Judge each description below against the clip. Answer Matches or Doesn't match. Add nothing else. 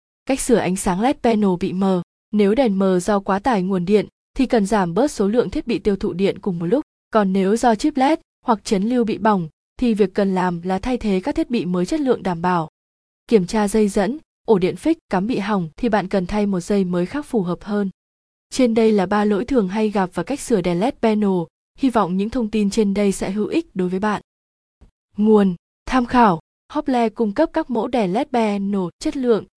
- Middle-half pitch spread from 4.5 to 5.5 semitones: Doesn't match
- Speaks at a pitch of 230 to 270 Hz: Doesn't match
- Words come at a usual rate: Matches